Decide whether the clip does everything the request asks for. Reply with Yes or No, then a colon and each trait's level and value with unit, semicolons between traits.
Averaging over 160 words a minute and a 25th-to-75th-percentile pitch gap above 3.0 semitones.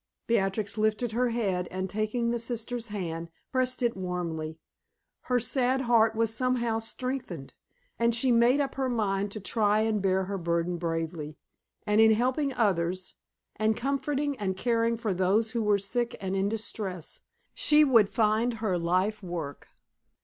No: average, 155 wpm; average, 4.1 semitones